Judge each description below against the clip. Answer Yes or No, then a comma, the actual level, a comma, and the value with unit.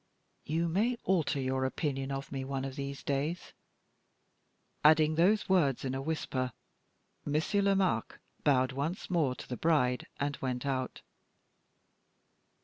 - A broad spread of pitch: No, average, 3.7 semitones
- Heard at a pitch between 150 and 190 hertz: No, medium, 140 Hz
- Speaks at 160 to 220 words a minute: No, slow, 135 wpm